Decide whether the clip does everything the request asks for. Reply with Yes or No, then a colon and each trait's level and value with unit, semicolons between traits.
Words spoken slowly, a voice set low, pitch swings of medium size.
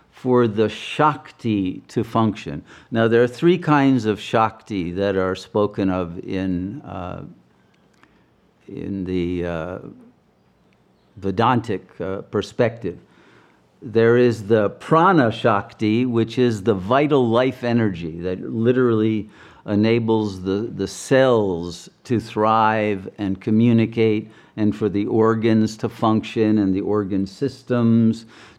Yes: slow, 115 wpm; low, 110 Hz; average, 3.2 semitones